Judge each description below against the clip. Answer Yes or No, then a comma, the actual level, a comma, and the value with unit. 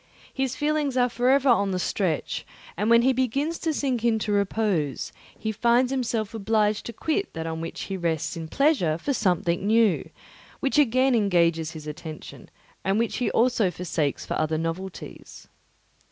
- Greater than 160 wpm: Yes, average, 170 wpm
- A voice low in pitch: No, high, 215 Hz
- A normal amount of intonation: No, wide, 6.8 semitones